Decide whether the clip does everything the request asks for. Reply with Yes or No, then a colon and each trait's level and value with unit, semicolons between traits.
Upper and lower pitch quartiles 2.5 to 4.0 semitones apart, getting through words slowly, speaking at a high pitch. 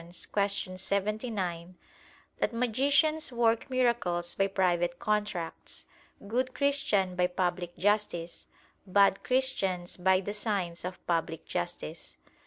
No: average, 4.6 semitones; slow, 100 wpm; high, 195 Hz